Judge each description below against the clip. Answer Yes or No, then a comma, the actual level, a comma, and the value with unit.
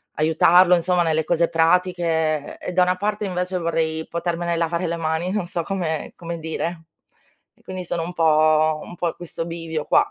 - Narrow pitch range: Yes, narrow, 1.9 semitones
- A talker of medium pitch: Yes, medium, 170 Hz